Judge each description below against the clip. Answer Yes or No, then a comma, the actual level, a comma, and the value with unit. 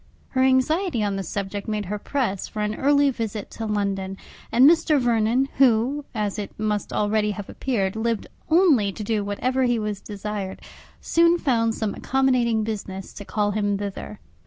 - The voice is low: No, high, 215 Hz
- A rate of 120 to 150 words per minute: No, average, 170 wpm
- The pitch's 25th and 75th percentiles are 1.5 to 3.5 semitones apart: No, average, 4.1 semitones